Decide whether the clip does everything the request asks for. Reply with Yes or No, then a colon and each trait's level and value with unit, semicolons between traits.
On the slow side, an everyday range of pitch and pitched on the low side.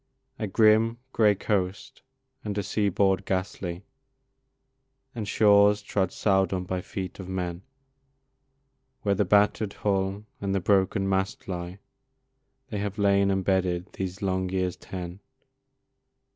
No: slow, 120 wpm; narrow, 1.7 semitones; very low, 95 Hz